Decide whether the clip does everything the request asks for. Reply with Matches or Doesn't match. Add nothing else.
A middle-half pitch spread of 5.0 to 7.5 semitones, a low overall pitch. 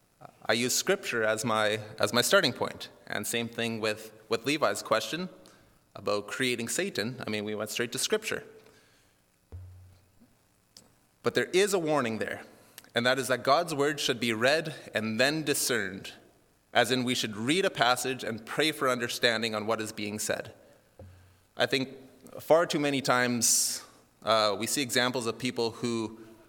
Doesn't match